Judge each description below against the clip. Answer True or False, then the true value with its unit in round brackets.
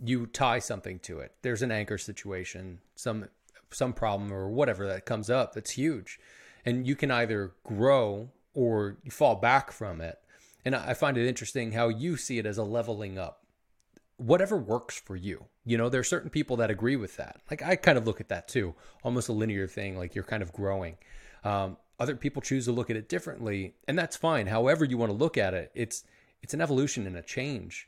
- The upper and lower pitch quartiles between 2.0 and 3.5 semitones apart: False (4.3 semitones)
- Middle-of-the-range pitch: False (115 Hz)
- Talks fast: True (215 wpm)